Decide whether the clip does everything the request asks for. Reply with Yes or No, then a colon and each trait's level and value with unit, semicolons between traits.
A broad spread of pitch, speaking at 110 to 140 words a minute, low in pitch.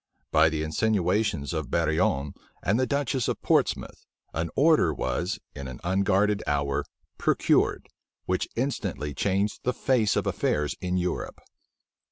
Yes: wide, 5.7 semitones; slow, 135 wpm; very low, 90 Hz